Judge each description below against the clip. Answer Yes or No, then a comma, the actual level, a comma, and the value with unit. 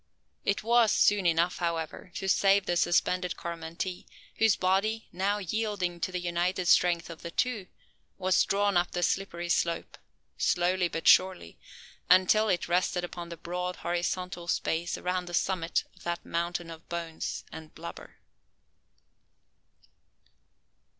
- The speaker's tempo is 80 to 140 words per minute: Yes, slow, 135 wpm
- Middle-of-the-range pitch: Yes, medium, 180 Hz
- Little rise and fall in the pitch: Yes, narrow, 1.8 semitones